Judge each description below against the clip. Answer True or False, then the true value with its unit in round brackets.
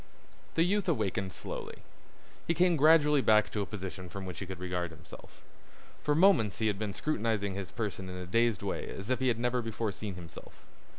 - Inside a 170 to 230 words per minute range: True (200 wpm)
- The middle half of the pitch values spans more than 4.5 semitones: True (5.4 semitones)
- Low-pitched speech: True (105 Hz)